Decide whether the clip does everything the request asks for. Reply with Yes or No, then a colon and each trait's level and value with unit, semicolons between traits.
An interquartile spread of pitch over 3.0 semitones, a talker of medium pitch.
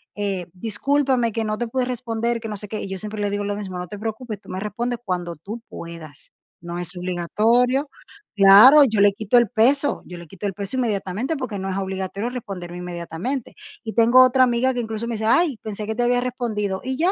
No: average, 4.2 semitones; high, 215 Hz